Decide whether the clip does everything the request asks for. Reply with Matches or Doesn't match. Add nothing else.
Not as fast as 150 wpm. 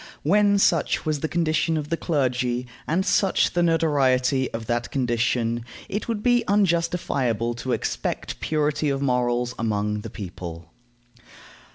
Matches